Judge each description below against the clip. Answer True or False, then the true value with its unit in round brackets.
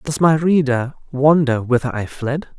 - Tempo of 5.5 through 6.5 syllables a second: False (4.4 syllables/s)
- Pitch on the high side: False (140 Hz)